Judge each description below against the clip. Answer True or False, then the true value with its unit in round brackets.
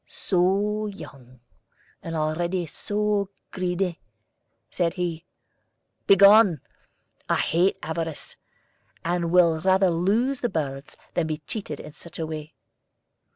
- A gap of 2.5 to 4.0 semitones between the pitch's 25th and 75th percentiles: True (3.6 semitones)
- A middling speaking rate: False (110 wpm)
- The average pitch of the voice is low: False (175 Hz)